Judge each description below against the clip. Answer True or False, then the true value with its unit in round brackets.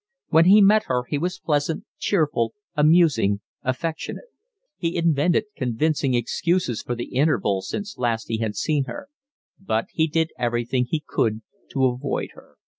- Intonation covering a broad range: True (5.7 semitones)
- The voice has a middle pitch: True (145 Hz)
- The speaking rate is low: False (150 wpm)